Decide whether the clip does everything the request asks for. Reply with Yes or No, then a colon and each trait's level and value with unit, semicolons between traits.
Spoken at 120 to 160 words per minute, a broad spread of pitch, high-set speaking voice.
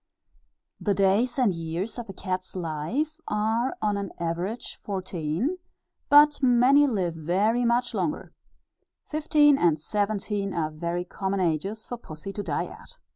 Yes: average, 140 wpm; wide, 5.7 semitones; high, 200 Hz